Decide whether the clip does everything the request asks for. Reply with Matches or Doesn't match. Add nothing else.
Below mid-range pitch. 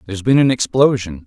Matches